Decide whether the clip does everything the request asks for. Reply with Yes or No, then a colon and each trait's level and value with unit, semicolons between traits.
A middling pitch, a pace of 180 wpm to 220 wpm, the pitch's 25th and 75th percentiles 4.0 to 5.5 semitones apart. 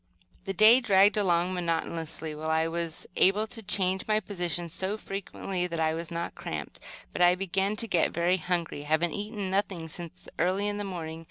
No: medium, 180 Hz; average, 185 wpm; average, 3.1 semitones